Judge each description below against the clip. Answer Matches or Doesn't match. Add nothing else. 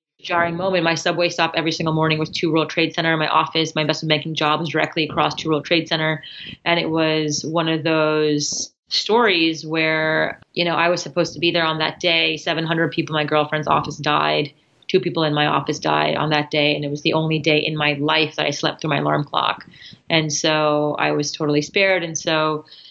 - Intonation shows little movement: Matches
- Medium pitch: Matches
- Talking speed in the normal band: Doesn't match